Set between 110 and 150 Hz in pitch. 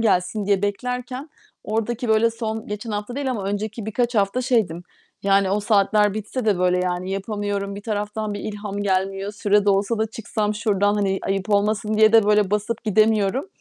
No: high, 210 Hz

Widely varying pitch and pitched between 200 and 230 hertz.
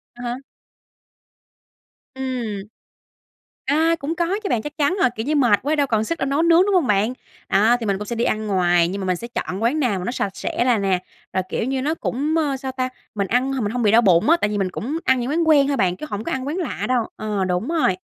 No: wide, 5.8 semitones; high, 245 Hz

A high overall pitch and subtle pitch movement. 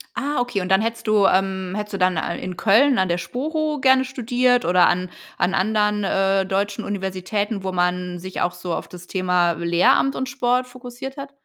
No: high, 200 Hz; average, 5.2 semitones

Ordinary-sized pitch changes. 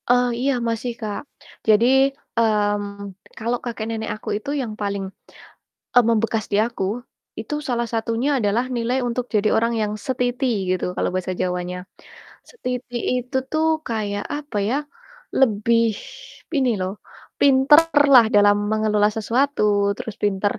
Yes: average, 3.3 semitones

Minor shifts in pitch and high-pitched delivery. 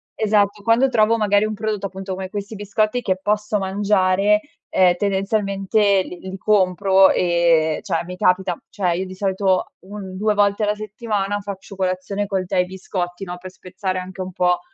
Yes: narrow, 2.0 semitones; high, 195 Hz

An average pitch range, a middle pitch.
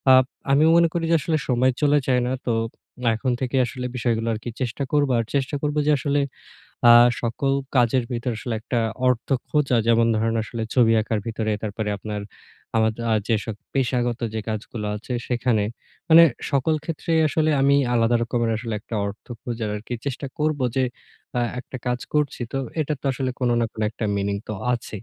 No: average, 3.4 semitones; low, 125 Hz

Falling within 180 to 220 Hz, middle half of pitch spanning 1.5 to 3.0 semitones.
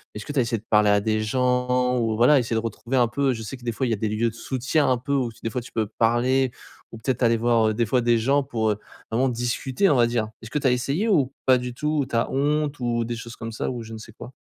No: low, 120 Hz; narrow, 2.5 semitones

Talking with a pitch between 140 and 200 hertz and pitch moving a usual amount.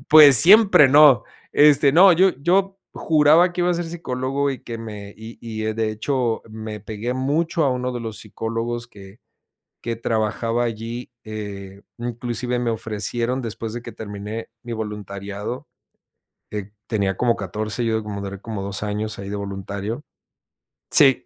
No: low, 115 Hz; average, 3.9 semitones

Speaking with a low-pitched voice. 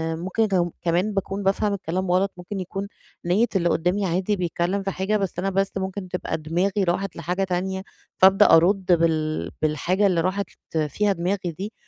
No: medium, 185 Hz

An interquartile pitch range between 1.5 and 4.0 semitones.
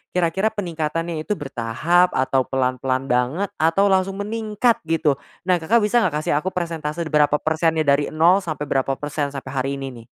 No: average, 4.6 semitones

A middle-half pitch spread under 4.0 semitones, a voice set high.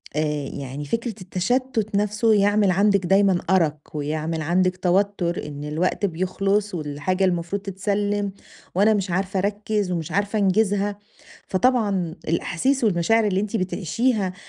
Yes: average, 3.1 semitones; high, 195 Hz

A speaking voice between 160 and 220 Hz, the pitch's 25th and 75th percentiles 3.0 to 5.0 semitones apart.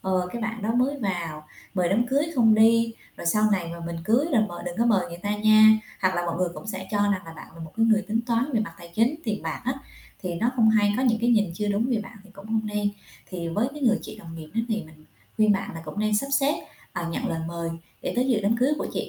Yes: high, 210 Hz; average, 4.3 semitones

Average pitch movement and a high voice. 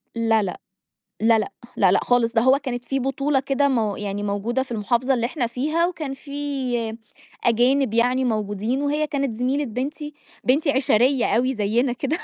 Yes: average, 3.4 semitones; very high, 250 Hz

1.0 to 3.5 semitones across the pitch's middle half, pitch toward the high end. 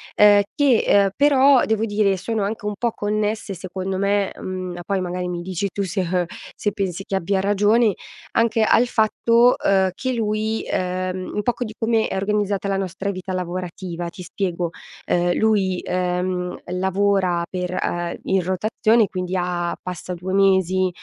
Yes: narrow, 2.6 semitones; high, 195 Hz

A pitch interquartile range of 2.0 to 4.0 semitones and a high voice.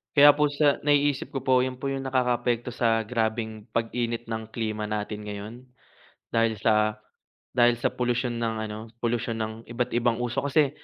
No: narrow, 2.5 semitones; low, 120 Hz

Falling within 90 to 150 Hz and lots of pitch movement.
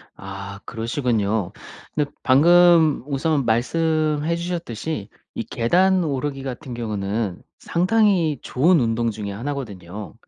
Yes: low, 135 Hz; wide, 6.4 semitones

